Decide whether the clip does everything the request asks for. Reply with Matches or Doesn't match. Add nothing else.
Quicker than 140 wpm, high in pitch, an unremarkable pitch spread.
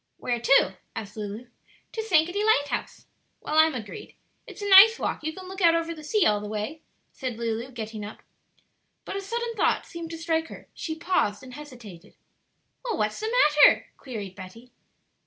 Doesn't match